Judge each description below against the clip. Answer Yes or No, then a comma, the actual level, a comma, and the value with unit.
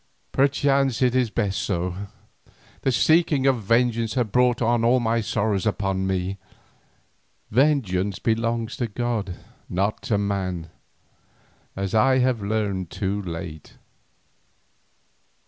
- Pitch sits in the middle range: No, low, 110 Hz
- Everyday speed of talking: No, slow, 115 wpm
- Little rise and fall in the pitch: No, average, 4.1 semitones